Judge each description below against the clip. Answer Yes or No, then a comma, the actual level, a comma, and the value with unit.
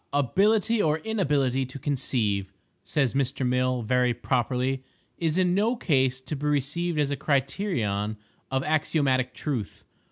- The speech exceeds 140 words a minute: No, slow, 135 wpm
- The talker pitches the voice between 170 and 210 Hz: No, low, 135 Hz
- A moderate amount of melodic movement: Yes, average, 3.5 semitones